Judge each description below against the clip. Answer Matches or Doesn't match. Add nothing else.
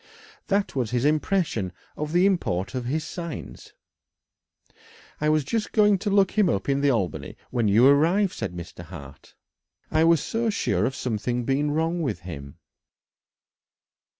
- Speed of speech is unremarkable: Matches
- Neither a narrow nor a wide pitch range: Doesn't match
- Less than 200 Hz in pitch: Matches